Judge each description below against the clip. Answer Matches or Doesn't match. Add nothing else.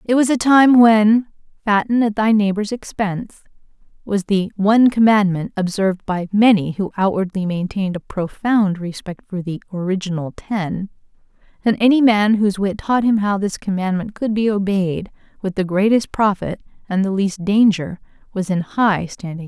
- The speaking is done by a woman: Matches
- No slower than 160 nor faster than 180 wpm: Matches